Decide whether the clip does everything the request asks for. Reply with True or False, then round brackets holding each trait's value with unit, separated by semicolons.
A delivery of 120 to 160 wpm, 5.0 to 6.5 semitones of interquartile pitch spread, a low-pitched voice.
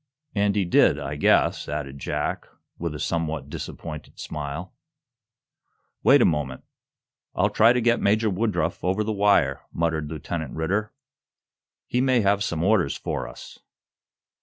True (140 wpm; 5.4 semitones; 85 Hz)